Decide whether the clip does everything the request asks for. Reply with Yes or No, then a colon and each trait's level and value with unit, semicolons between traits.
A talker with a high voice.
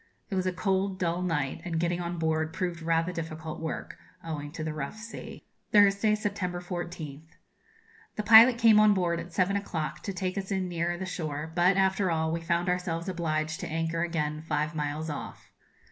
No: medium, 170 Hz